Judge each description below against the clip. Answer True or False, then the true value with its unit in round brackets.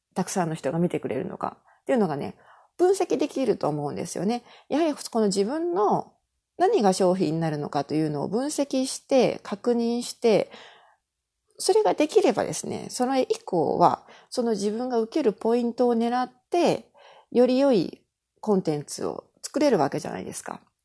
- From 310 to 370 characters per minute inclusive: True (335 characters per minute)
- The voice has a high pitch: True (235 Hz)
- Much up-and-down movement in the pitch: True (6.2 semitones)